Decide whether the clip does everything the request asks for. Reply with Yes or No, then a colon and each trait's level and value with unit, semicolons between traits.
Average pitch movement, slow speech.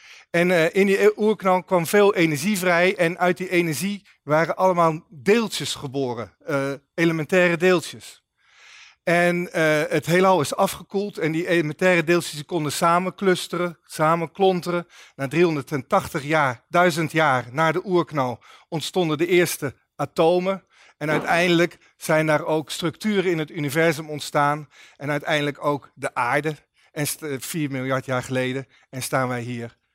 Yes: average, 3.5 semitones; slow, 130 wpm